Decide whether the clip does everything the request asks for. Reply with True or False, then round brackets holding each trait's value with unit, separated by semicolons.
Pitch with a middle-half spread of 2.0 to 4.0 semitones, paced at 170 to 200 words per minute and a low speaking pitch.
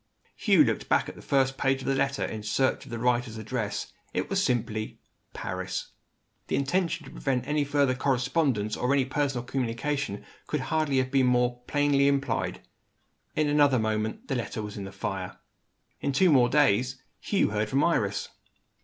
True (3.6 semitones; 175 wpm; 130 Hz)